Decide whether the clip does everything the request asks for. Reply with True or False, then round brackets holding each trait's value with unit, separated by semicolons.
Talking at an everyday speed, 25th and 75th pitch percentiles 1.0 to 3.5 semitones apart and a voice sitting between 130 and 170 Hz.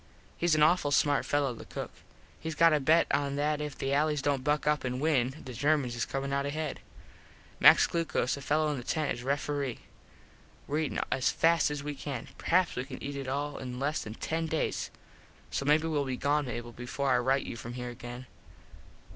False (215 wpm; 2.7 semitones; 140 Hz)